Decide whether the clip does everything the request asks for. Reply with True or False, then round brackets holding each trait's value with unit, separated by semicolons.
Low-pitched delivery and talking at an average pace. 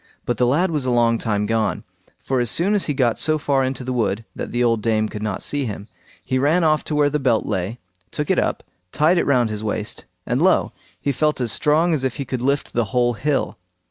False (125 Hz; 245 wpm)